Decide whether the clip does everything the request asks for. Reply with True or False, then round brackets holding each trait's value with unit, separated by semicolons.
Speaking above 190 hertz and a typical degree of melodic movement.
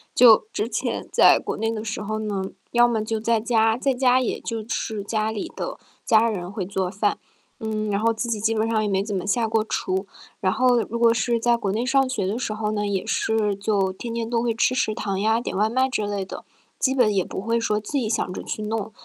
False (220 Hz; 2.0 semitones)